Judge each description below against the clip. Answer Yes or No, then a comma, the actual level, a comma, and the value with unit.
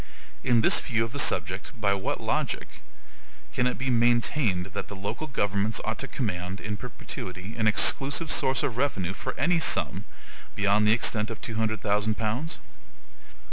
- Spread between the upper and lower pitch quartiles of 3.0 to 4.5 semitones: Yes, average, 3.6 semitones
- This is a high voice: No, low, 110 Hz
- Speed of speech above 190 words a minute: No, average, 170 wpm